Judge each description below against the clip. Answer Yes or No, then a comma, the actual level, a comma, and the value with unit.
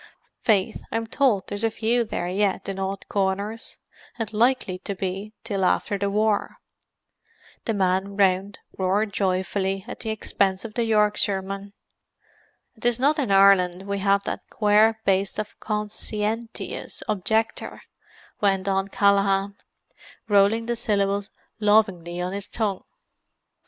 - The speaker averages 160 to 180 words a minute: No, average, 140 wpm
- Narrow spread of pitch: Yes, narrow, 2.1 semitones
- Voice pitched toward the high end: Yes, high, 200 Hz